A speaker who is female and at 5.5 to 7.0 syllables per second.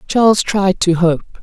No: female; 4.4 syllables/s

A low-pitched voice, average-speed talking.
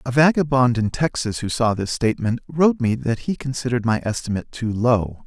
Yes: low, 125 Hz; average, 195 wpm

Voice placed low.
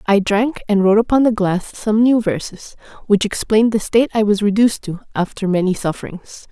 No: high, 210 Hz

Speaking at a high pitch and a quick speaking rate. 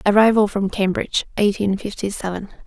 No: high, 200 Hz; slow, 135 wpm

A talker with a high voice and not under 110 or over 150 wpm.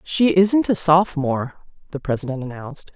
No: medium, 160 Hz; average, 140 wpm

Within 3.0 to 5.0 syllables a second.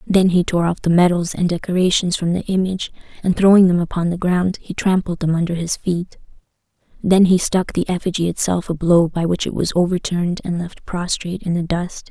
No: 5.6 syllables/s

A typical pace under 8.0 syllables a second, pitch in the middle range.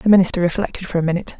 No: 8.9 syllables/s; medium, 180 Hz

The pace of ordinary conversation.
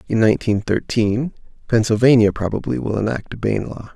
Yes: average, 150 wpm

